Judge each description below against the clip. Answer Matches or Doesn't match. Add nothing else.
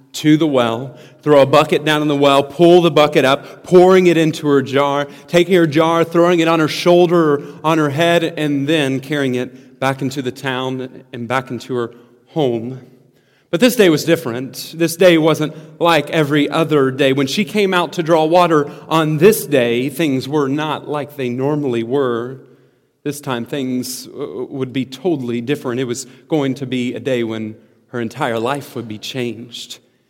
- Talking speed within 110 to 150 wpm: Doesn't match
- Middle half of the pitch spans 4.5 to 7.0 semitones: Doesn't match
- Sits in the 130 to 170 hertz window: Matches